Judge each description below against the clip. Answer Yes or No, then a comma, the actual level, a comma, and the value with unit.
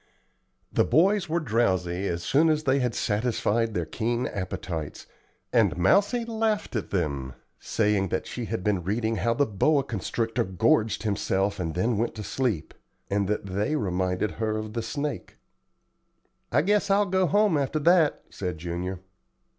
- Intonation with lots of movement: Yes, wide, 7.8 semitones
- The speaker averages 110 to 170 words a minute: Yes, average, 160 wpm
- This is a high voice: No, low, 110 Hz